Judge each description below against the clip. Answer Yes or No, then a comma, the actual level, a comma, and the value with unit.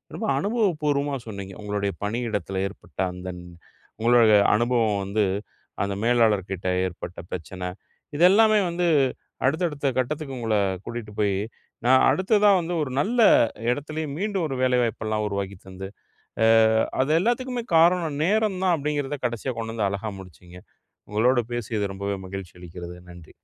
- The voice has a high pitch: No, low, 120 Hz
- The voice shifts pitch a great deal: Yes, wide, 7.6 semitones